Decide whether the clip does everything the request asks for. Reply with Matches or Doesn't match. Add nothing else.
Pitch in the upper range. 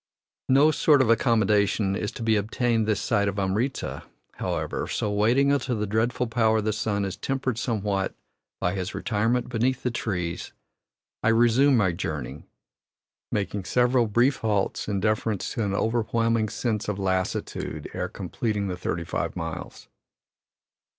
Doesn't match